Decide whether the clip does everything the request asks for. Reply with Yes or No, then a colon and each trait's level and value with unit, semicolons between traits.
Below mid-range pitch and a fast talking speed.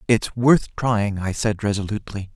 No: low, 105 Hz; average, 155 wpm